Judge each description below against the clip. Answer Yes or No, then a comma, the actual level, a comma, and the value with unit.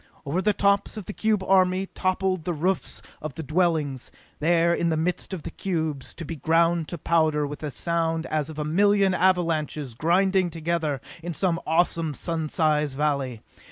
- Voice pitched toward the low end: No, medium, 165 Hz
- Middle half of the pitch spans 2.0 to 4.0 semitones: Yes, average, 3.2 semitones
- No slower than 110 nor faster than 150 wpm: No, average, 180 wpm